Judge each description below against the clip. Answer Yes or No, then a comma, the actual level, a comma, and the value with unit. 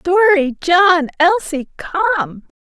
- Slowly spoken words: Yes, slow, 70 wpm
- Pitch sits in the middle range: No, very high, 335 Hz